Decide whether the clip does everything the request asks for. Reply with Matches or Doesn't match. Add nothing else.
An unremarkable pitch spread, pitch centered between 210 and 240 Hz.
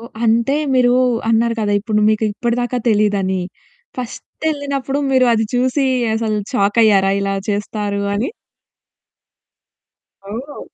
Matches